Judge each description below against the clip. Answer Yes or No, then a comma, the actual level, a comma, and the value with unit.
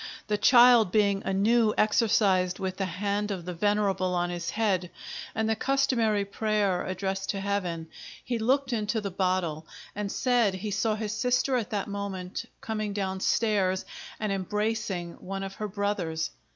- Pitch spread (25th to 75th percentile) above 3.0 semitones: No, narrow, 2.5 semitones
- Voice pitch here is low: No, high, 200 Hz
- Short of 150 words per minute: No, average, 160 wpm